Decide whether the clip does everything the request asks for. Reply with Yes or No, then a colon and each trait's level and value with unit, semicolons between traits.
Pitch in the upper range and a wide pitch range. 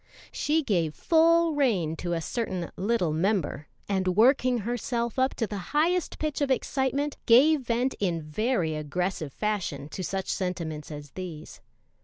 Yes: high, 205 Hz; wide, 7.6 semitones